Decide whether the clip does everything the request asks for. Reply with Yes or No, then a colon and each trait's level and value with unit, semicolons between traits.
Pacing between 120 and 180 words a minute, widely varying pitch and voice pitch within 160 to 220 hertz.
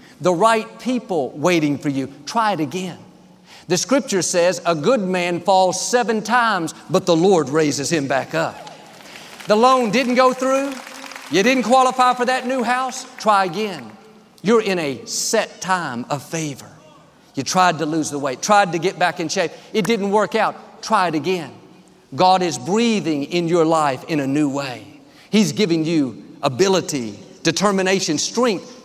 Yes: average, 170 wpm; wide, 6.0 semitones; medium, 185 Hz